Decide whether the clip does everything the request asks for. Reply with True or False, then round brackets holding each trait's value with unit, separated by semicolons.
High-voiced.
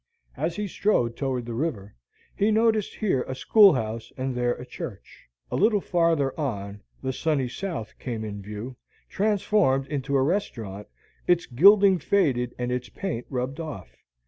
False (135 Hz)